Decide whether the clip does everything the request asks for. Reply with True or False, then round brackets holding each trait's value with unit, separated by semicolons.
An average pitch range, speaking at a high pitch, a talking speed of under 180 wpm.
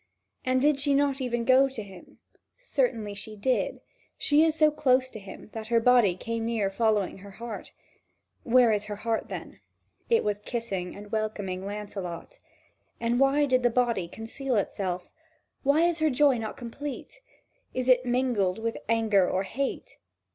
True (4.2 semitones; 230 Hz; 165 wpm)